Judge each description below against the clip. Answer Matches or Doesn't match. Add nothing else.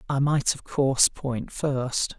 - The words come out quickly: Doesn't match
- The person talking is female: Doesn't match